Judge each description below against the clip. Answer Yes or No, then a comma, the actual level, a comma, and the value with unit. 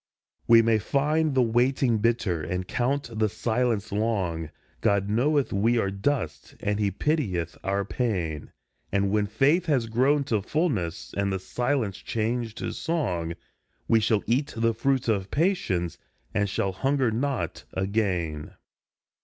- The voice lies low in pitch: Yes, low, 110 Hz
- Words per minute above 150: No, average, 145 wpm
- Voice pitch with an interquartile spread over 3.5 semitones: Yes, average, 5.1 semitones